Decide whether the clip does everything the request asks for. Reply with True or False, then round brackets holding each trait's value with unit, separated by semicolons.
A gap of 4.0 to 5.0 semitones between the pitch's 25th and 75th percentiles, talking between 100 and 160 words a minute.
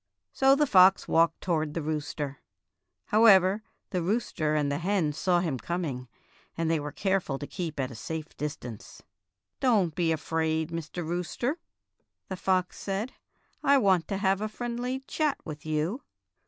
True (4.5 semitones; 155 wpm)